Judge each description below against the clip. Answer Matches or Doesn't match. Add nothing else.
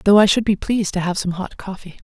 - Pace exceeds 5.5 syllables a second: Matches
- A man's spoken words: Doesn't match